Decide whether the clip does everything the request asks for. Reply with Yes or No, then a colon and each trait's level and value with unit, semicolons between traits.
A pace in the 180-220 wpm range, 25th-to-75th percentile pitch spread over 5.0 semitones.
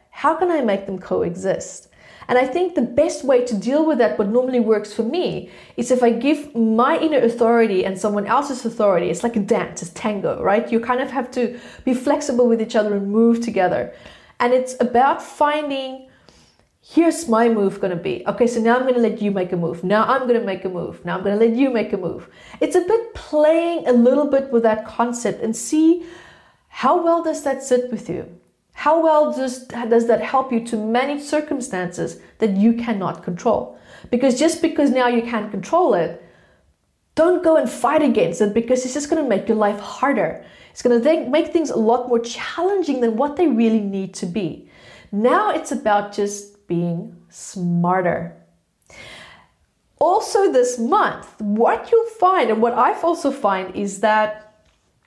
Yes: average, 200 wpm; wide, 5.6 semitones